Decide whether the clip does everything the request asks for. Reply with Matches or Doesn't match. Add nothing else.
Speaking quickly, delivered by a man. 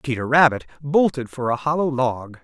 Doesn't match